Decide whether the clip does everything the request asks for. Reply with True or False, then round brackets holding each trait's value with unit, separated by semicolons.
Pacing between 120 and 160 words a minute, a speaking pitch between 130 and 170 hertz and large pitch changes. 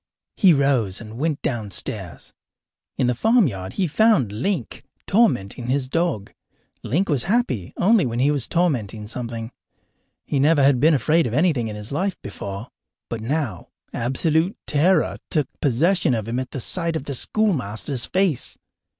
True (150 wpm; 135 Hz; 6.5 semitones)